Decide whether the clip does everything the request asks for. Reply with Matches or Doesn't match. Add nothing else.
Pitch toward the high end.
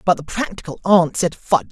Doesn't match